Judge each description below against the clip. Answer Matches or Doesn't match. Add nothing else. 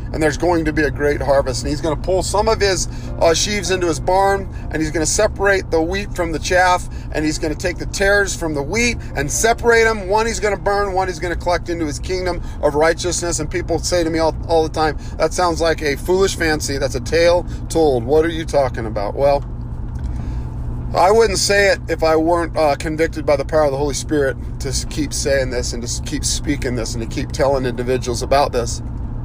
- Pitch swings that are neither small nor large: Matches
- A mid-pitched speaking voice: Matches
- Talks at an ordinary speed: Doesn't match